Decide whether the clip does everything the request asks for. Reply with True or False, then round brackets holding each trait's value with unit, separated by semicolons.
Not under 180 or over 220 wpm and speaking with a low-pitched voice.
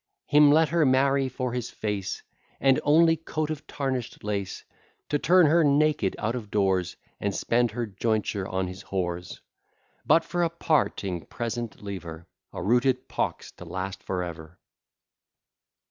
False (155 wpm; 120 Hz)